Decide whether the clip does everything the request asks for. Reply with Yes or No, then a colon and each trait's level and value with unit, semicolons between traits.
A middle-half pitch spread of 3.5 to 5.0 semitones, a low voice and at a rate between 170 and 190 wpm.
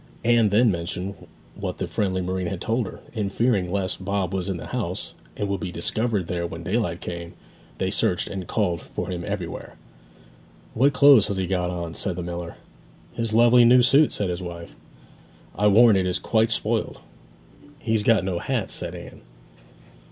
Yes: average, 4.0 semitones; very low, 95 Hz; average, 180 wpm